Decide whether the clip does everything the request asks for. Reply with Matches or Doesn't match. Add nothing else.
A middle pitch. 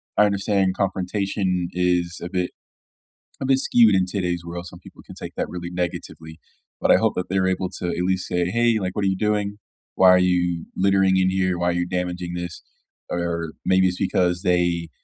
Doesn't match